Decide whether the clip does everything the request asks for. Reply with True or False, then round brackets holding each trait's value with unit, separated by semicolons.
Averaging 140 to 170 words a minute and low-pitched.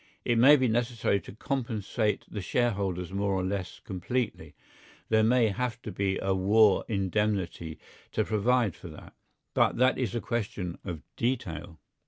True (155 wpm; 105 Hz)